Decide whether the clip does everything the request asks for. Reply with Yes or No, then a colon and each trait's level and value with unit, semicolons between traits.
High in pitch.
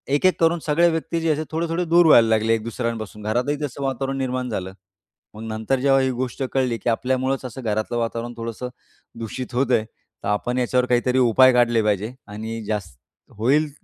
No: low, 125 Hz